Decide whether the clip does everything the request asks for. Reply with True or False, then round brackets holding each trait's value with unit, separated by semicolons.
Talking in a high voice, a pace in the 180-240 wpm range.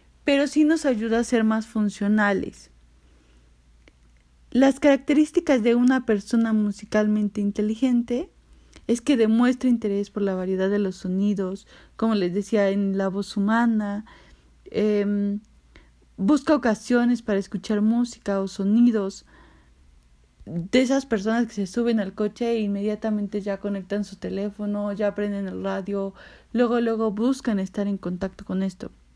False (210 Hz; 135 wpm)